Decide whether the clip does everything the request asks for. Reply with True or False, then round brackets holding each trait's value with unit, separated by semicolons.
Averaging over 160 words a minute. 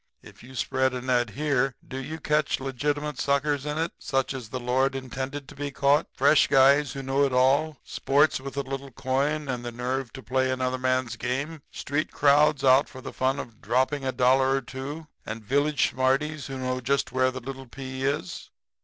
True (200 wpm)